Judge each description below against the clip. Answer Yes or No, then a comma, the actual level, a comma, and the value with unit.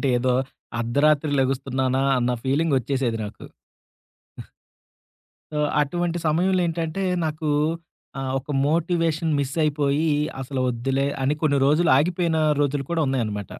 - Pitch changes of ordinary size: Yes, average, 3.5 semitones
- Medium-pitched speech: Yes, medium, 145 Hz